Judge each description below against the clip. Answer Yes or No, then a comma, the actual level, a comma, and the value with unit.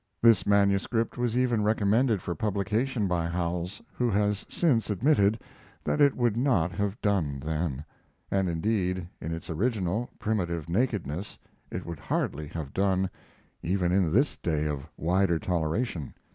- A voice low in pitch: Yes, very low, 95 Hz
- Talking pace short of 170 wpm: Yes, average, 145 wpm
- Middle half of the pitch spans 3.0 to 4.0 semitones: No, average, 4.7 semitones